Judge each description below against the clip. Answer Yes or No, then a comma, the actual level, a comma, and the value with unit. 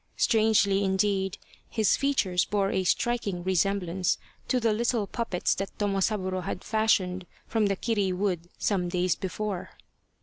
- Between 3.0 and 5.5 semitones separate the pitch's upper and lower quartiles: No, narrow, 2.6 semitones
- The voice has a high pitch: Yes, high, 195 Hz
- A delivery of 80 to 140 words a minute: Yes, slow, 135 wpm